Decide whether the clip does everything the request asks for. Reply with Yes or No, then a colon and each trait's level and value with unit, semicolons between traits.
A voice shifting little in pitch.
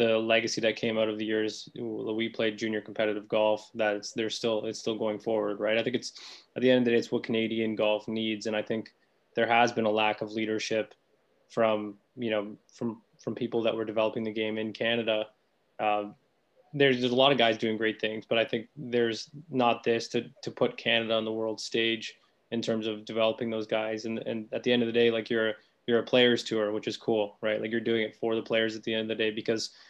Yes: narrow, 1.1 semitones